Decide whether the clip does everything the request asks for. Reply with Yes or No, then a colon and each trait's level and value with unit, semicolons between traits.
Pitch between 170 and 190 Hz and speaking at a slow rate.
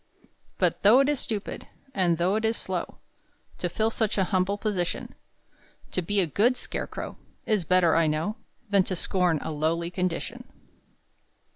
No: medium, 185 Hz; average, 160 wpm